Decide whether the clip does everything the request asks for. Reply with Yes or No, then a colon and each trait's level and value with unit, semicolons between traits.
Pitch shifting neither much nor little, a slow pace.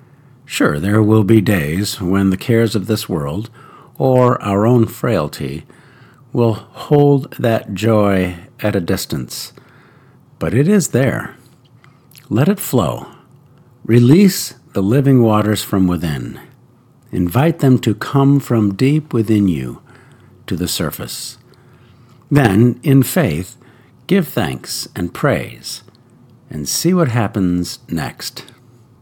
Yes: average, 4.2 semitones; slow, 120 wpm